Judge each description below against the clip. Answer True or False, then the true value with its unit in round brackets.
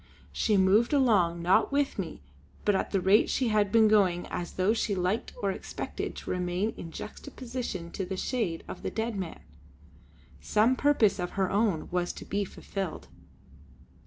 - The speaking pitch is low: False (200 Hz)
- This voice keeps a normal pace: True (170 wpm)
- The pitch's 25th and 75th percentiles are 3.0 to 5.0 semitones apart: True (3.6 semitones)